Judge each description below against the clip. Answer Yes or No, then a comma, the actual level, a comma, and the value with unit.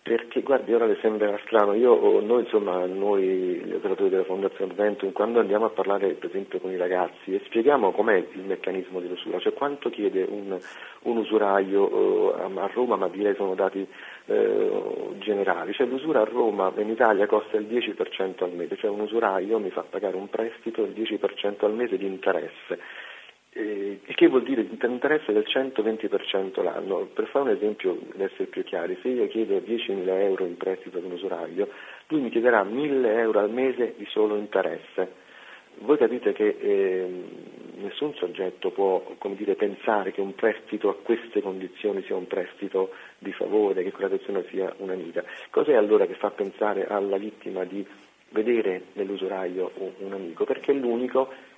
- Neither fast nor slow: No, fast, 175 wpm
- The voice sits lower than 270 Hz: No, very high, 350 Hz